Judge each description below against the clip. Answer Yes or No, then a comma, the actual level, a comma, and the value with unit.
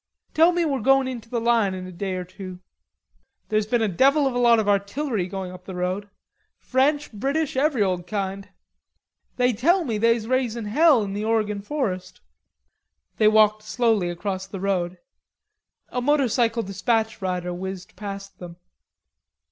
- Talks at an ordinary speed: Yes, average, 160 wpm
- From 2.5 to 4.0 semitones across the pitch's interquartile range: No, average, 4.5 semitones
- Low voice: No, high, 215 Hz